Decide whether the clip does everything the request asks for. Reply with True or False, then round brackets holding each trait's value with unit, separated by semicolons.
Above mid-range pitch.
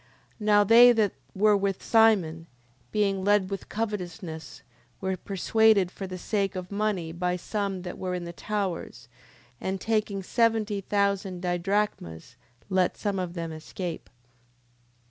True (195 Hz)